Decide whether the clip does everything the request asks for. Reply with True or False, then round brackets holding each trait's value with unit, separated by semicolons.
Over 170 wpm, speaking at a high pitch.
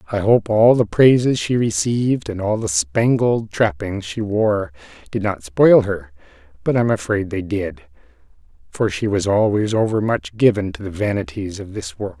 False (180 wpm; 110 Hz)